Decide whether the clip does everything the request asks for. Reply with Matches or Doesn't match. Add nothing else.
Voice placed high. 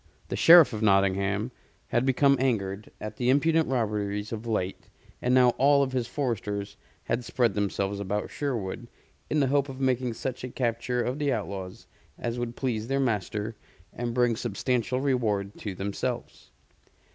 Doesn't match